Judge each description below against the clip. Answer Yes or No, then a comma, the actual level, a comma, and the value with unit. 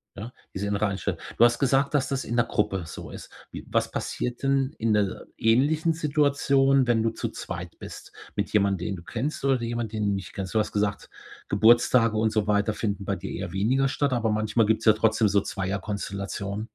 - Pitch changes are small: No, average, 4.0 semitones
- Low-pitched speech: Yes, low, 110 Hz